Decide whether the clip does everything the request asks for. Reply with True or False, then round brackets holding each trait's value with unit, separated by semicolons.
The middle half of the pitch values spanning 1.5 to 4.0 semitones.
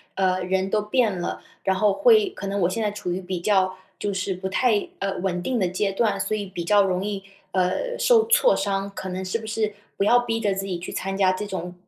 True (2.4 semitones)